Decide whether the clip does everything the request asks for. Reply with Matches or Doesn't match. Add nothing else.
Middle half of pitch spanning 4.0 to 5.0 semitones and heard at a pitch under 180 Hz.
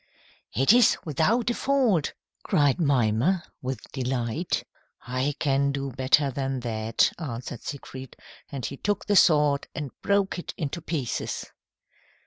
Matches